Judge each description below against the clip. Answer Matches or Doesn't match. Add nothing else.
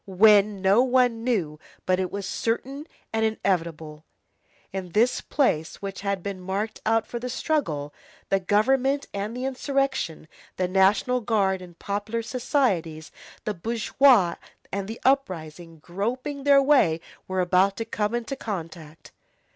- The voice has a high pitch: Matches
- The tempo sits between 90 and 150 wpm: Matches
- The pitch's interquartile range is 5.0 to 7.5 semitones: Matches